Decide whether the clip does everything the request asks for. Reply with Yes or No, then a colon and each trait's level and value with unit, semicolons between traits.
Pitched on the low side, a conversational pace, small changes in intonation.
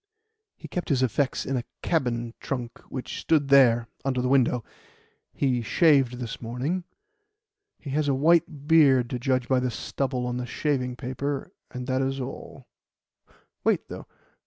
Yes: low, 130 Hz; average, 160 wpm; narrow, 2.2 semitones